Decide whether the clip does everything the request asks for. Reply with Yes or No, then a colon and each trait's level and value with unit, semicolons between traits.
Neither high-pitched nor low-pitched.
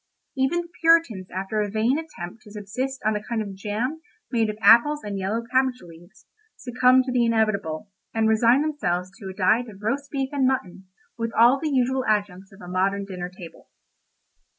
No: high, 220 Hz